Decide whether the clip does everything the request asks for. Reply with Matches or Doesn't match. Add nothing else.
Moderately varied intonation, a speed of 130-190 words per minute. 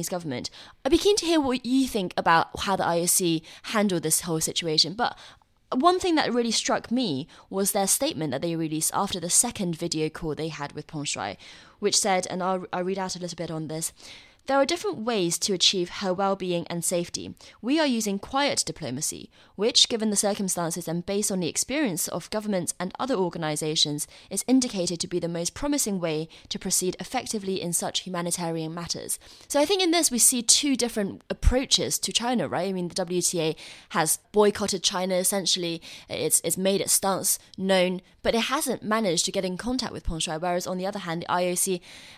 Doesn't match